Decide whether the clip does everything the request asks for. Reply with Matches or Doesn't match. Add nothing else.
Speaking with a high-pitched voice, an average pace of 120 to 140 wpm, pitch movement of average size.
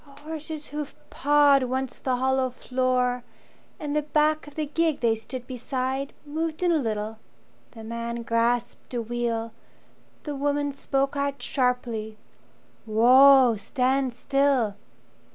Matches